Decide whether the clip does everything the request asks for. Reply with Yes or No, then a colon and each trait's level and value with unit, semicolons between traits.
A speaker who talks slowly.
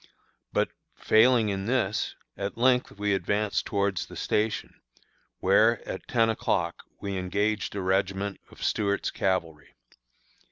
Yes: slow, 125 wpm